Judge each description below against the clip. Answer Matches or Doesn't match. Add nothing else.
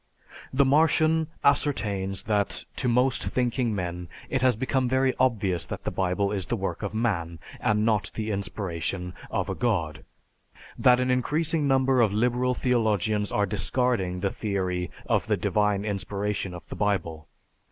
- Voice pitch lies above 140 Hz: Doesn't match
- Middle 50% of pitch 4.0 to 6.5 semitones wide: Matches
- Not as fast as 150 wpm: Doesn't match